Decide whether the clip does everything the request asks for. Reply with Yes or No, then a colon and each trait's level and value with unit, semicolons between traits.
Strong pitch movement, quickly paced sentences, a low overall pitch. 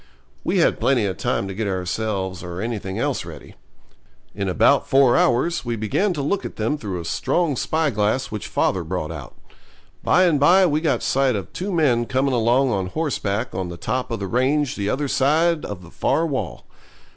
No: wide, 7.0 semitones; average, 195 wpm; low, 120 Hz